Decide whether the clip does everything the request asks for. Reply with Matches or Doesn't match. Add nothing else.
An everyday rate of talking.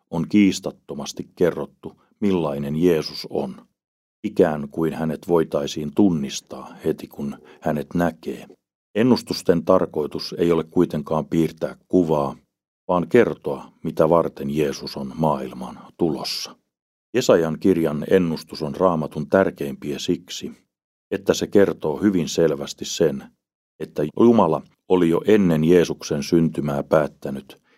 Matches